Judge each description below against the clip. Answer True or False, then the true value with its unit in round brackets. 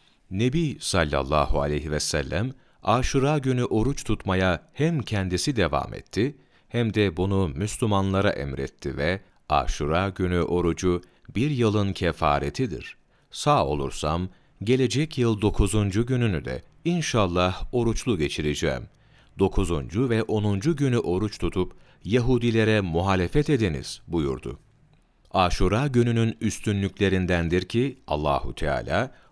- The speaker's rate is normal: True (105 wpm)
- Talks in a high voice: False (100 Hz)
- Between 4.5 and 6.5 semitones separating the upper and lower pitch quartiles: True (5.6 semitones)